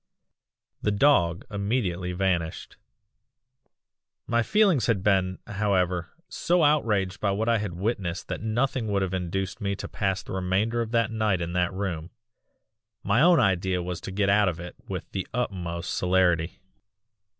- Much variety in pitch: No, average, 3.5 semitones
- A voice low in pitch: Yes, very low, 95 Hz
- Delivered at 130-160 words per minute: Yes, average, 155 wpm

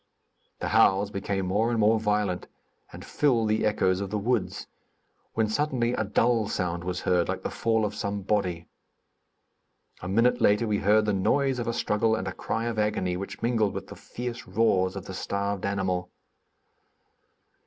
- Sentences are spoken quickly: No, average, 175 wpm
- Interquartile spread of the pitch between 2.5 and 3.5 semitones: Yes, average, 3.0 semitones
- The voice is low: Yes, low, 105 Hz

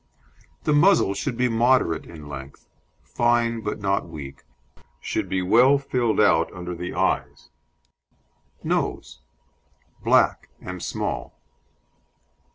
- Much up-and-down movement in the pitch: Yes, wide, 6.3 semitones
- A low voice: Yes, low, 100 Hz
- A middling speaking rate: No, slow, 110 wpm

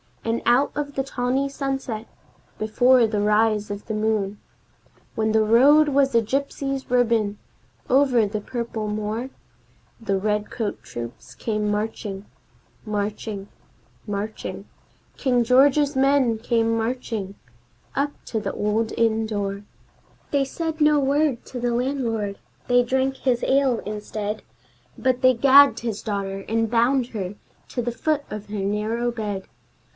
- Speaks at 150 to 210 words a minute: No, slow, 135 wpm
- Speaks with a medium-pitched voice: No, high, 230 Hz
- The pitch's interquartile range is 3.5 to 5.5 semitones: Yes, average, 3.9 semitones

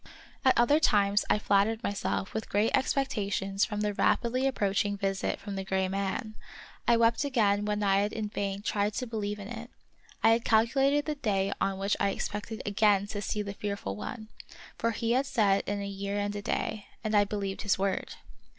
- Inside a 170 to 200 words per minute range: Yes, average, 195 wpm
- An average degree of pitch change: No, narrow, 2.3 semitones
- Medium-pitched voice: No, high, 205 Hz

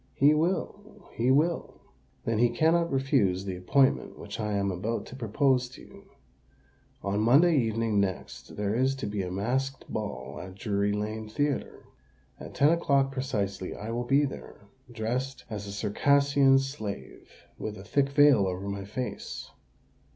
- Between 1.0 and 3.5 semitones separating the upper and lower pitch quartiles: No, average, 5.1 semitones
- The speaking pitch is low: Yes, low, 120 Hz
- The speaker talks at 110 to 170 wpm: Yes, average, 155 wpm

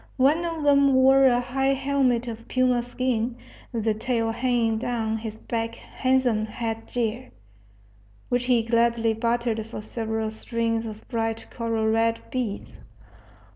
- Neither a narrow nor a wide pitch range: No, narrow, 2.2 semitones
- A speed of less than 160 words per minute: Yes, average, 140 wpm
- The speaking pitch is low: No, high, 235 Hz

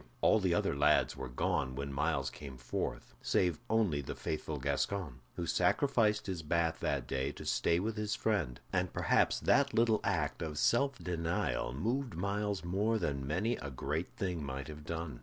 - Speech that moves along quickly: No, average, 175 wpm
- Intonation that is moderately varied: No, wide, 6.4 semitones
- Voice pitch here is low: Yes, very low, 85 Hz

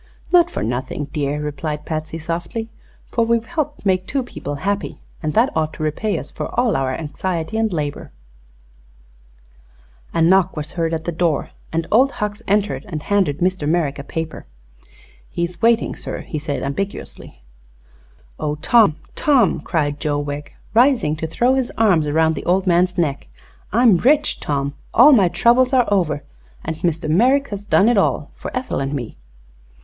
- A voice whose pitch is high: No, medium, 170 Hz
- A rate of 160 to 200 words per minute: Yes, average, 170 wpm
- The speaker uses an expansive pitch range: Yes, wide, 6.7 semitones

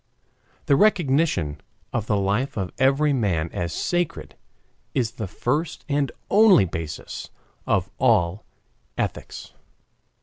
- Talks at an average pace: No, slow, 110 wpm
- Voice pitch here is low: Yes, low, 120 Hz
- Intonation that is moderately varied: No, wide, 8.0 semitones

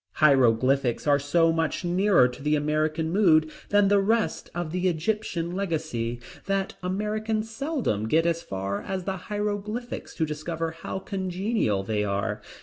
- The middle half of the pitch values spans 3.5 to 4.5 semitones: No, wide, 5.5 semitones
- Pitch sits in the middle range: Yes, medium, 165 Hz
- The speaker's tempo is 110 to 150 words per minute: Yes, average, 145 wpm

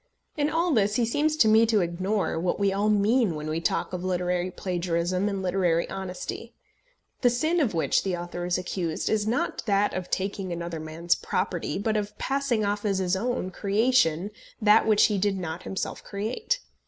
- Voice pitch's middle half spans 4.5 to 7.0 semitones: No, average, 3.5 semitones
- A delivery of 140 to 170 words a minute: No, average, 190 wpm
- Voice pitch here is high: Yes, high, 195 Hz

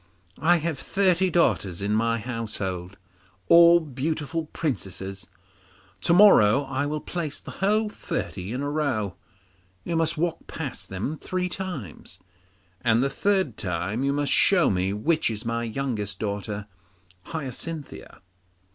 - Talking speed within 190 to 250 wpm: No, slow, 135 wpm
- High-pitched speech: No, medium, 140 Hz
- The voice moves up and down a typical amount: No, wide, 7.6 semitones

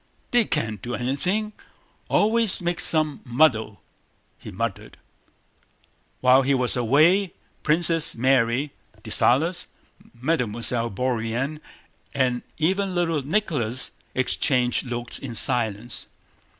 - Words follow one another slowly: Yes, slow, 100 wpm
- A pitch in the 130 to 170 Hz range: Yes, low, 135 Hz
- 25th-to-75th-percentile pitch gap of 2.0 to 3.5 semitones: No, wide, 5.6 semitones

